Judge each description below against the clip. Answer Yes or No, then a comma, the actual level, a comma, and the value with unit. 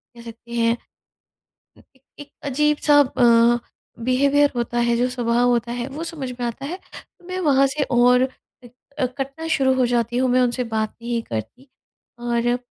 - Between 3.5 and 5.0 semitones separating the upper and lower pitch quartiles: No, narrow, 2.6 semitones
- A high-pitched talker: Yes, high, 245 Hz